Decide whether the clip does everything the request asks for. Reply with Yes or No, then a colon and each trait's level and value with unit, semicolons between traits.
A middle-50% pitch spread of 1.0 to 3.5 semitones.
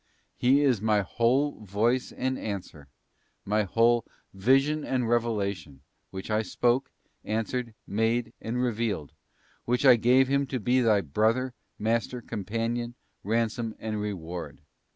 Yes: average, 3.0 semitones